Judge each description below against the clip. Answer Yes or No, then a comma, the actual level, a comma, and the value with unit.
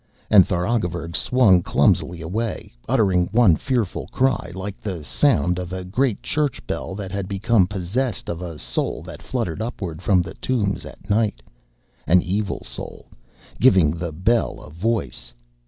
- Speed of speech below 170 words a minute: Yes, average, 155 wpm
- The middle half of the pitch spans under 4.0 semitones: No, average, 4.4 semitones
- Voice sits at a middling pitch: No, very low, 95 Hz